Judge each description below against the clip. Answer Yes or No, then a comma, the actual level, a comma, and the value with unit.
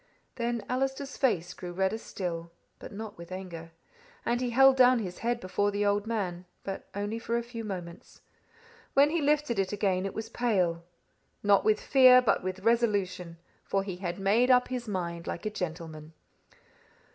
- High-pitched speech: Yes, high, 205 Hz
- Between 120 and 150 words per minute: No, average, 175 wpm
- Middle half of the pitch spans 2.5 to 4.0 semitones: No, average, 4.7 semitones